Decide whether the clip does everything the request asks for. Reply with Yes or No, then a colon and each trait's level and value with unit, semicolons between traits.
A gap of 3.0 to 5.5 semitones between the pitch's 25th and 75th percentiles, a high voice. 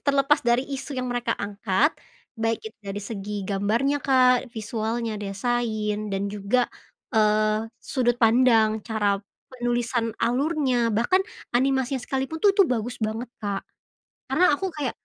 Yes: average, 3.5 semitones; high, 235 Hz